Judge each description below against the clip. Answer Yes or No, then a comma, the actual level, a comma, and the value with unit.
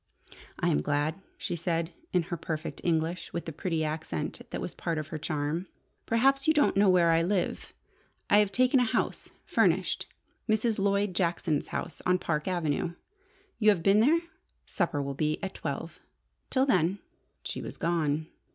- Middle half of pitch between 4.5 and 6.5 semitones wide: No, average, 4.1 semitones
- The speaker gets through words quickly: No, average, 175 wpm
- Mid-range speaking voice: Yes, medium, 170 Hz